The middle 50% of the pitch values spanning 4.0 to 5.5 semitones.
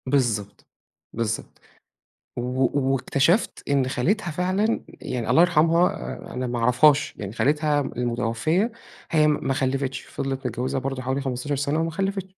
Yes: average, 4.4 semitones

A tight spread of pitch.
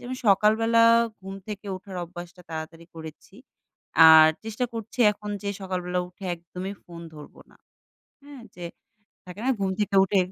No: average, 3.4 semitones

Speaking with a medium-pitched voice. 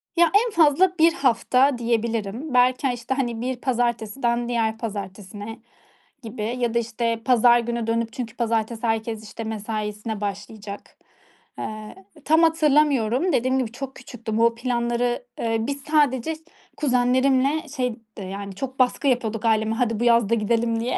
No: high, 235 Hz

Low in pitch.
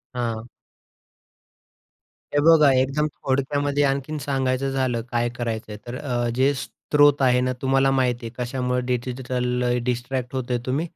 Yes: low, 130 Hz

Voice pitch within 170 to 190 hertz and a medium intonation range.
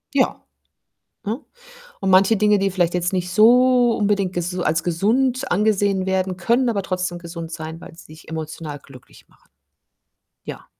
Yes: medium, 185 Hz; average, 3.7 semitones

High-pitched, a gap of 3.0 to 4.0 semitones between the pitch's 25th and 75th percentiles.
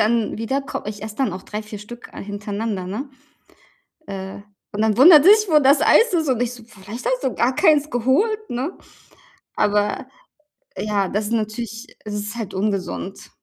No: high, 225 Hz; average, 4.6 semitones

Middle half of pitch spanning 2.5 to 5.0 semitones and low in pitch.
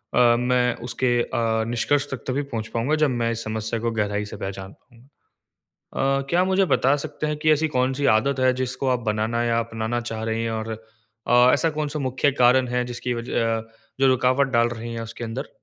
Yes: average, 2.8 semitones; low, 120 Hz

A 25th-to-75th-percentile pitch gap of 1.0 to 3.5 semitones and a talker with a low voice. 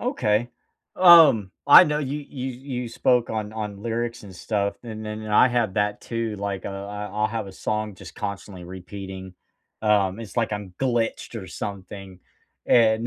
Yes: average, 2.7 semitones; low, 105 Hz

